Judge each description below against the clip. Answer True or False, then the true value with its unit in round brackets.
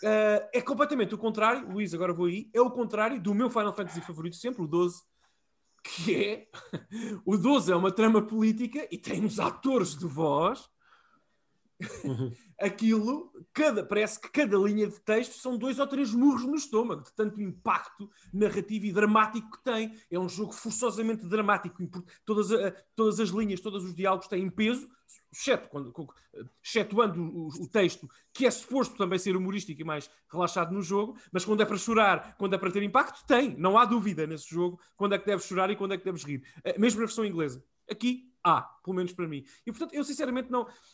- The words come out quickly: True (195 wpm)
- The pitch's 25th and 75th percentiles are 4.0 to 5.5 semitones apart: True (4.3 semitones)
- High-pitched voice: True (210 Hz)